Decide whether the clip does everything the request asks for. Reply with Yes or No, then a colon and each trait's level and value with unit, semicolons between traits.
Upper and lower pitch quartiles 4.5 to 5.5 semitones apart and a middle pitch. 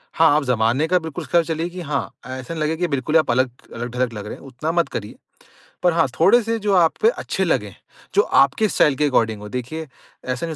Yes: average, 4.9 semitones; medium, 155 Hz